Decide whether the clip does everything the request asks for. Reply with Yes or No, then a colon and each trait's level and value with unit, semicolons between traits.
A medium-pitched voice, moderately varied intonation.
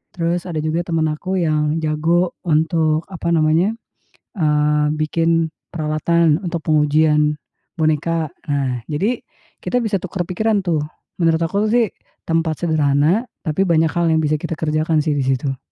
No: medium, 160 Hz; narrow, 2.0 semitones